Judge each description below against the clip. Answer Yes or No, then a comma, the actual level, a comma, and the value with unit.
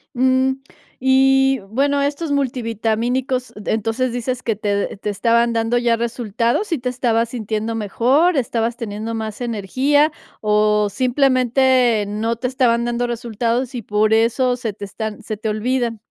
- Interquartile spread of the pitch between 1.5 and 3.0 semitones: Yes, average, 2.7 semitones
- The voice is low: No, high, 235 Hz